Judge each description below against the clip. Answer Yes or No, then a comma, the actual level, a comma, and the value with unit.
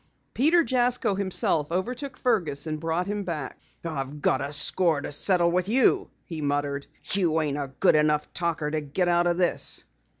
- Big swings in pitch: No, average, 4.4 semitones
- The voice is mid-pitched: Yes, medium, 170 Hz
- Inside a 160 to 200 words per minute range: Yes, average, 175 wpm